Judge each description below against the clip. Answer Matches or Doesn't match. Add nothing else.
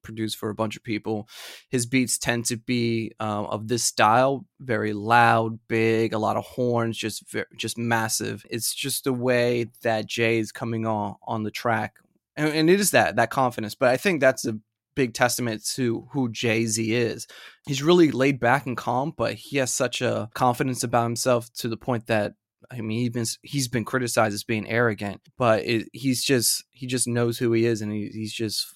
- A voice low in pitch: Matches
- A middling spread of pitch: Doesn't match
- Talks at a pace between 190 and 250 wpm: Matches